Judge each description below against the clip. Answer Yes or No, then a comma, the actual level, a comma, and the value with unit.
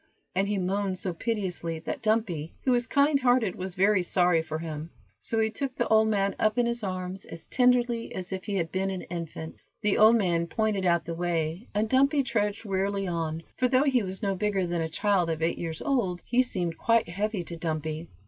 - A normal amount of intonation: Yes, average, 4.5 semitones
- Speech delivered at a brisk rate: Yes, fast, 215 wpm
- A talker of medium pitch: No, high, 195 Hz